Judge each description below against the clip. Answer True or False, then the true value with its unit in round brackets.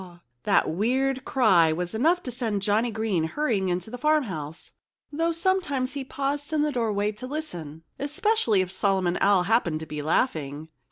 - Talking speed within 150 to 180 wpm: True (165 wpm)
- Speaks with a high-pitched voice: True (220 Hz)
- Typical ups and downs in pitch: False (7.7 semitones)